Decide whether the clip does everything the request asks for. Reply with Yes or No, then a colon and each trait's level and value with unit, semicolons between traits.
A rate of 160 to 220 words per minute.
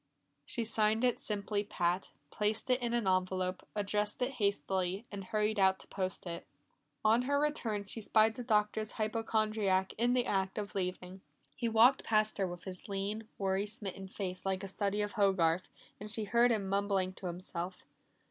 Yes: average, 175 wpm